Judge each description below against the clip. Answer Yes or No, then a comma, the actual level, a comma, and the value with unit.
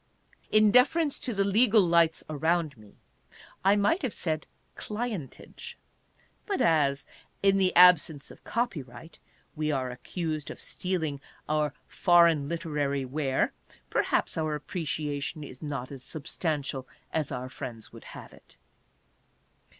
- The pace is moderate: No, slow, 130 wpm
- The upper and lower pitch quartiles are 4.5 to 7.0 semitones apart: Yes, average, 4.9 semitones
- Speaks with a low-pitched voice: No, medium, 155 Hz